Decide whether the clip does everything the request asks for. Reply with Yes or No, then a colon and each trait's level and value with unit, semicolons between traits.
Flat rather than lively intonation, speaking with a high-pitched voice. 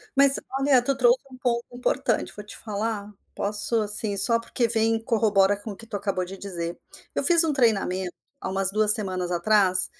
No: average, 3.3 semitones; high, 210 Hz